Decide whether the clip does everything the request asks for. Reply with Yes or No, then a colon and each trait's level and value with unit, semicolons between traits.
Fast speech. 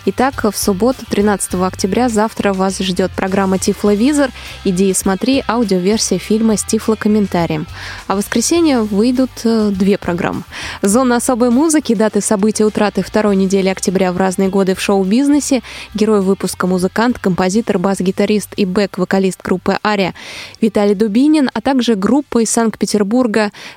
No: average, 135 wpm